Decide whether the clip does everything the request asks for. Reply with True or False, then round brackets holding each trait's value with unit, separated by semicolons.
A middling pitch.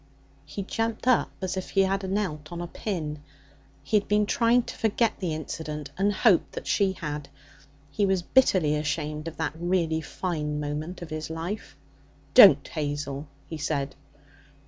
True (165 Hz)